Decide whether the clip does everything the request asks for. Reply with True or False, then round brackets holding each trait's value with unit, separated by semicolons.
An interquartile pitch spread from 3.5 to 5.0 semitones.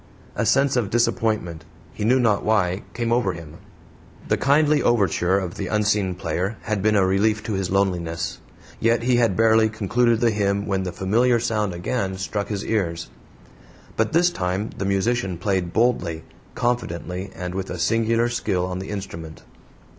True (4.0 semitones)